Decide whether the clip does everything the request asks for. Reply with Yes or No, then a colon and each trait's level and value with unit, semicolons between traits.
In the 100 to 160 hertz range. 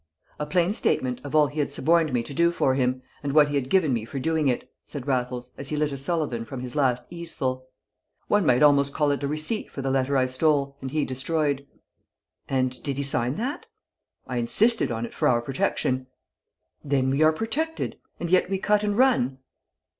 Yes: medium, 140 Hz